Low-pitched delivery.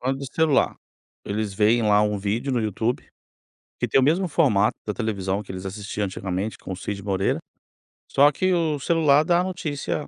Yes: low, 110 Hz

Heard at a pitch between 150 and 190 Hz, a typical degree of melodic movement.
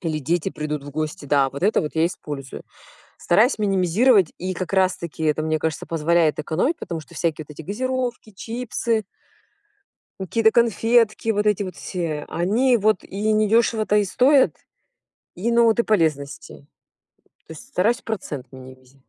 No: medium, 185 Hz; wide, 6.2 semitones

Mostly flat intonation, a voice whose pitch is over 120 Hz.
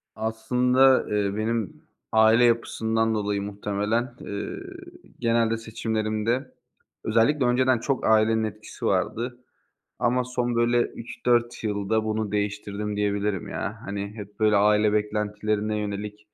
No: narrow, 2.2 semitones; low, 110 Hz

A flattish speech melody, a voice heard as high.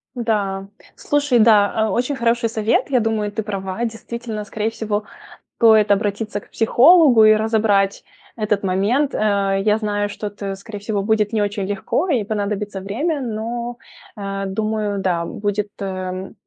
Yes: narrow, 2.0 semitones; high, 210 Hz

